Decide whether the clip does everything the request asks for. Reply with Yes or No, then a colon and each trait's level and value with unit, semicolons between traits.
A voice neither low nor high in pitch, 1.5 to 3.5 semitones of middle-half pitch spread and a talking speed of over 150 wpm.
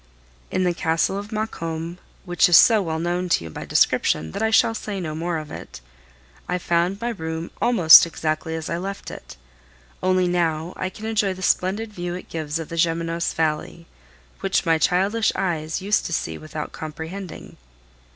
Yes: medium, 175 Hz; average, 3.0 semitones; average, 180 wpm